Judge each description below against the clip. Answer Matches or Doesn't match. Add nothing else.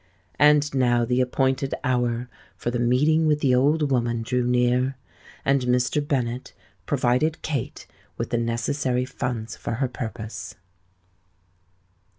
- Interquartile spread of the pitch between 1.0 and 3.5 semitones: Matches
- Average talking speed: Doesn't match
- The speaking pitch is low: Matches